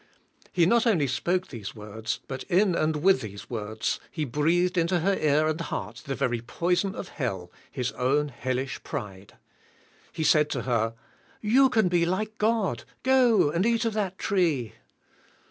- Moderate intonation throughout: No, wide, 7.4 semitones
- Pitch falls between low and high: Yes, medium, 155 Hz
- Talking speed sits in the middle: Yes, average, 165 wpm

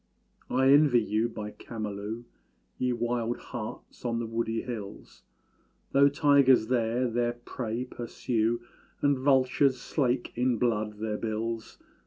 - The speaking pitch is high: No, low, 120 Hz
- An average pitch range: No, narrow, 2.3 semitones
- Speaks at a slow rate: Yes, slow, 125 wpm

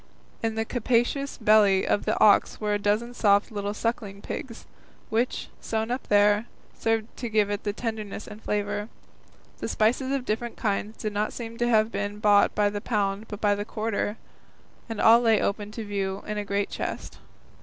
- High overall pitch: Yes, high, 215 Hz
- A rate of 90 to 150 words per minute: No, average, 185 wpm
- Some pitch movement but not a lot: No, narrow, 1.7 semitones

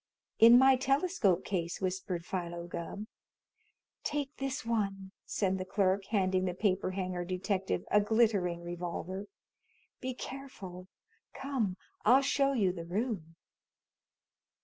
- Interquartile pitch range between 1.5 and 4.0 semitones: No, average, 4.7 semitones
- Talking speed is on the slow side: Yes, slow, 120 wpm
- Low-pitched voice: No, high, 195 Hz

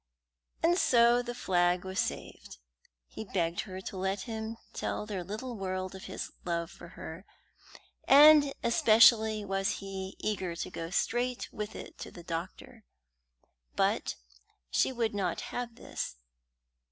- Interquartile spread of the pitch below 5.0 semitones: Yes, average, 4.0 semitones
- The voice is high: Yes, high, 200 Hz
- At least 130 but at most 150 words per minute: Yes, average, 140 wpm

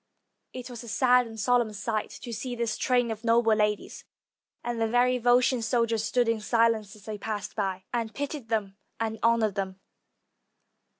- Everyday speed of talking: Yes, average, 175 wpm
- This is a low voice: No, high, 230 Hz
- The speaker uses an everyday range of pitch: No, narrow, 2.1 semitones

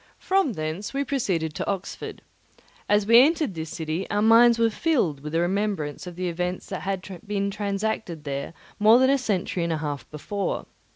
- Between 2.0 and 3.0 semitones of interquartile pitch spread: No, average, 5.2 semitones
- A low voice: No, high, 195 Hz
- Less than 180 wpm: No, average, 185 wpm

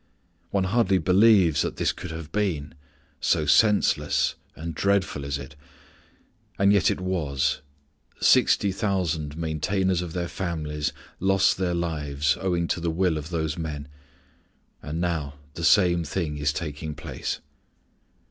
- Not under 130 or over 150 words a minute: Yes, average, 140 wpm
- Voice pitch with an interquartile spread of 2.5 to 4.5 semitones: Yes, average, 3.7 semitones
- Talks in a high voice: No, very low, 85 Hz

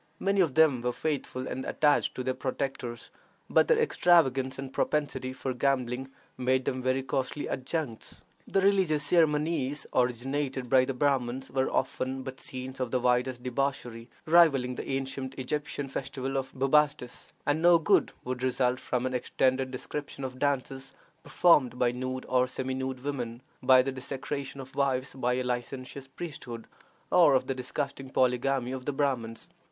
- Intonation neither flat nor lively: No, narrow, 1.8 semitones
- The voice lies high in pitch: No, low, 130 Hz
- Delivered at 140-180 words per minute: Yes, average, 160 wpm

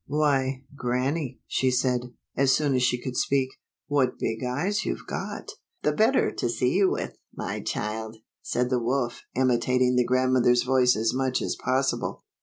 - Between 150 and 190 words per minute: Yes, average, 175 wpm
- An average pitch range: No, narrow, 1.6 semitones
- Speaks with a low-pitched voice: Yes, low, 130 Hz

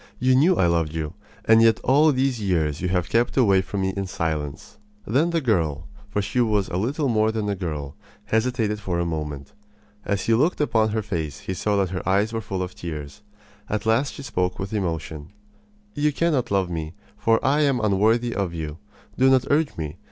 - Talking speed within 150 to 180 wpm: No, fast, 205 wpm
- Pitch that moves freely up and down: Yes, wide, 5.8 semitones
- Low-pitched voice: Yes, low, 100 Hz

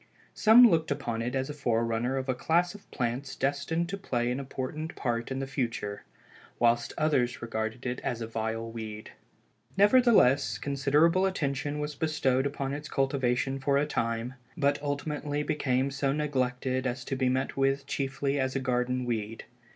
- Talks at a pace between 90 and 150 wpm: No, average, 165 wpm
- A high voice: No, low, 135 Hz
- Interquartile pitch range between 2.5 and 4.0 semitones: Yes, average, 2.9 semitones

